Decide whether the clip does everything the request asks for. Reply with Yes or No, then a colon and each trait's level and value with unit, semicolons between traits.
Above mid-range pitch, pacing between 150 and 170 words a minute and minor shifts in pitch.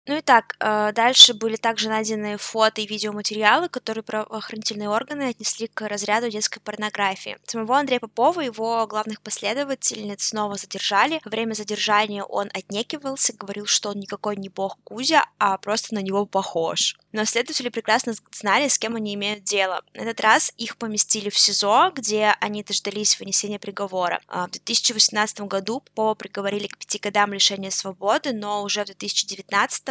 Yes: high, 215 Hz; fast, 160 wpm; narrow, 2.0 semitones